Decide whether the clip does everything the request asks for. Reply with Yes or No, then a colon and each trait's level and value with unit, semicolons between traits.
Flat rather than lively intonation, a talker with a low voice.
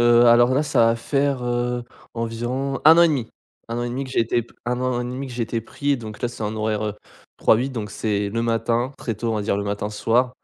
Yes: narrow, 2.2 semitones; low, 120 Hz